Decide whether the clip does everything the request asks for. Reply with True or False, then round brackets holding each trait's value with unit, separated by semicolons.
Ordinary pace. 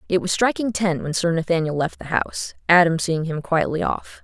False (210 wpm)